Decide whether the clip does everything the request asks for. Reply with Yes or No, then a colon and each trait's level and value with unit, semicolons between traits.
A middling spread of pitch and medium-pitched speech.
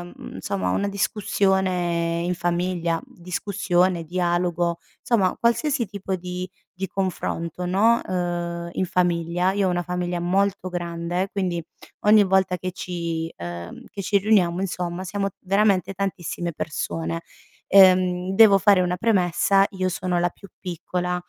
No: narrow, 1.9 semitones; medium, 180 Hz